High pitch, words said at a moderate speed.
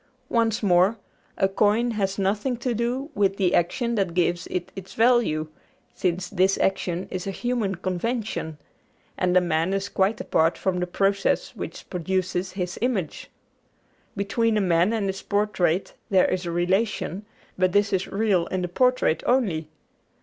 Yes: high, 195 Hz; average, 160 wpm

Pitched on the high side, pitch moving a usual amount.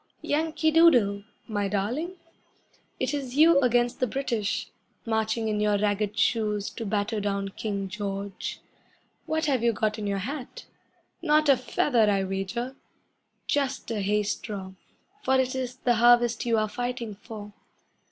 Yes: high, 225 Hz; average, 3.9 semitones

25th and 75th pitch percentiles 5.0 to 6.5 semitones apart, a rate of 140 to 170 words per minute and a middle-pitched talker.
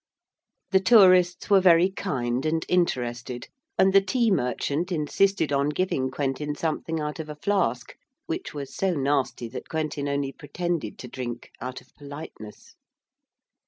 Yes: wide, 5.4 semitones; average, 145 wpm; medium, 150 Hz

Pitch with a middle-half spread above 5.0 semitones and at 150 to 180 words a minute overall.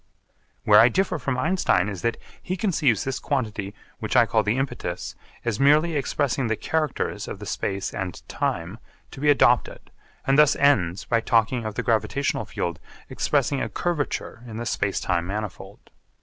Yes: wide, 5.5 semitones; average, 170 wpm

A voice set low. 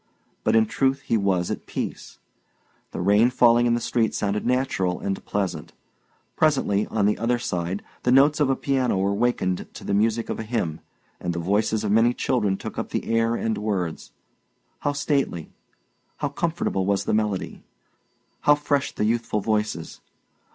Yes: low, 110 Hz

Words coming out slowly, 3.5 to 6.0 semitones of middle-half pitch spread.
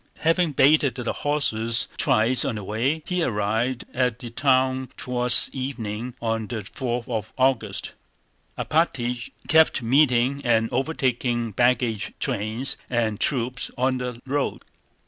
No: slow, 125 wpm; average, 2.7 semitones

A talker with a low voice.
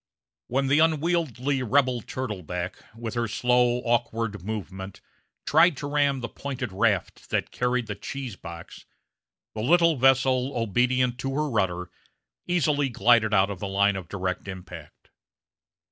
Yes: low, 120 Hz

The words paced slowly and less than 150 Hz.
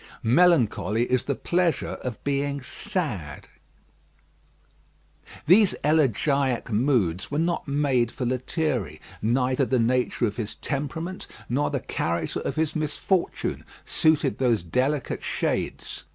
Yes: slow, 115 wpm; low, 135 Hz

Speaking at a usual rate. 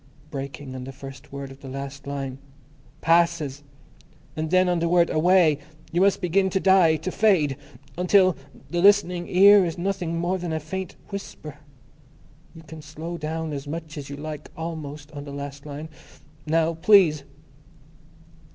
Yes: average, 165 wpm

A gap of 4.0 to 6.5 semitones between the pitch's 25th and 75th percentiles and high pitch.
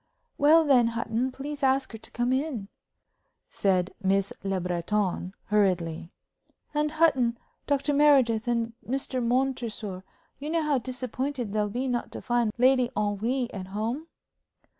Yes: average, 4.5 semitones; high, 240 Hz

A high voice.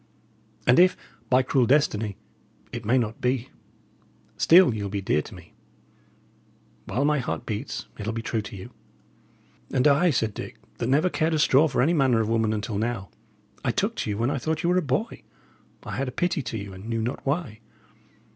No: low, 125 Hz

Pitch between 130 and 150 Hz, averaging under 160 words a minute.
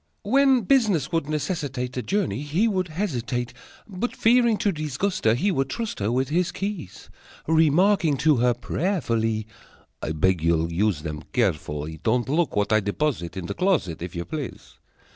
No: medium, 140 Hz; average, 165 wpm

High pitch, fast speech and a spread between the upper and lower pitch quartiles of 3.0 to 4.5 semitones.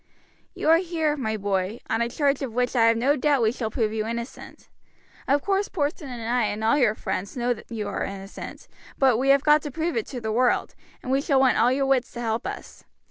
Yes: very high, 250 Hz; fast, 240 wpm; average, 4.1 semitones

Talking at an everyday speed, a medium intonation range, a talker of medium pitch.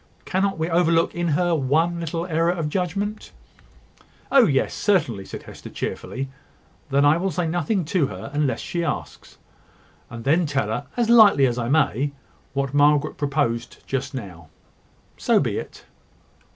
Yes: average, 155 wpm; average, 4.1 semitones; medium, 155 Hz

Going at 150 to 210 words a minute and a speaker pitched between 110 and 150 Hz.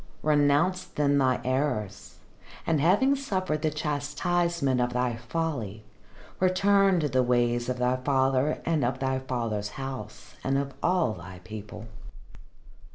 No: slow, 135 wpm; low, 135 Hz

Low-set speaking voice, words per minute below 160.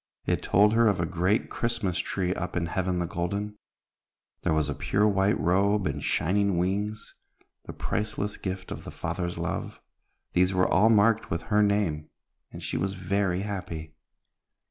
No: very low, 95 Hz; average, 165 wpm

